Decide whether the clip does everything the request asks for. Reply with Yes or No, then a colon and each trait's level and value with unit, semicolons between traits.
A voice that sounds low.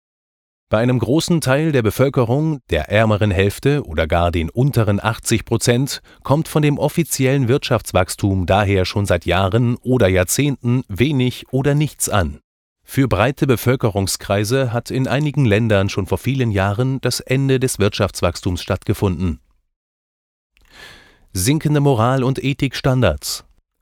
Yes: low, 120 Hz